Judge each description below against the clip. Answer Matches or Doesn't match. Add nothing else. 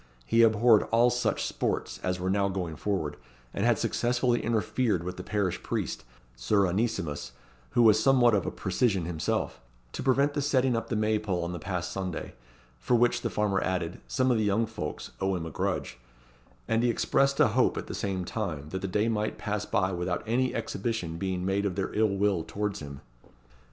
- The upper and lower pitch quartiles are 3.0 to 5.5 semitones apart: Matches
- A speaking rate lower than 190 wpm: Doesn't match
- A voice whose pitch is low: Matches